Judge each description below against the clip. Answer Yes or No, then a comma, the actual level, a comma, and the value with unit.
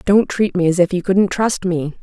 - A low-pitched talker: No, medium, 185 Hz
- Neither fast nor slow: No, fast, 265 wpm